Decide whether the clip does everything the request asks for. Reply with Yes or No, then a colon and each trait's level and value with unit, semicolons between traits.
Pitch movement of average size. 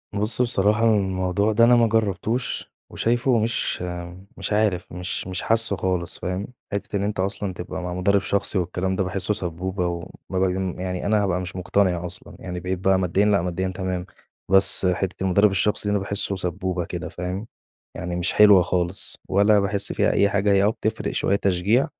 No: narrow, 2.2 semitones